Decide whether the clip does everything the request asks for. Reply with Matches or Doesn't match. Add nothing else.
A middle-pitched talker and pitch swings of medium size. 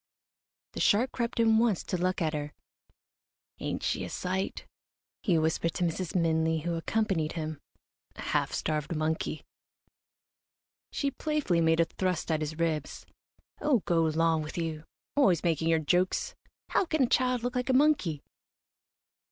Doesn't match